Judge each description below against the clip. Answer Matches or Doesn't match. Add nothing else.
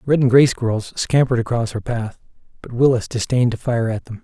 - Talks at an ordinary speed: Doesn't match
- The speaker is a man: Matches